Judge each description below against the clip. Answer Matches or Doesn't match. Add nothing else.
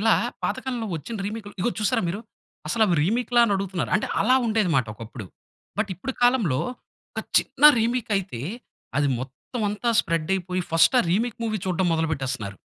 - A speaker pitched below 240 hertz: Matches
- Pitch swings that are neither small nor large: Doesn't match